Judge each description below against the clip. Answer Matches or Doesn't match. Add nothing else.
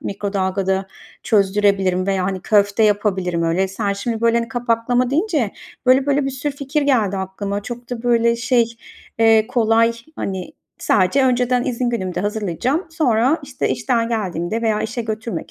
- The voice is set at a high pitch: Matches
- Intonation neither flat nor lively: Matches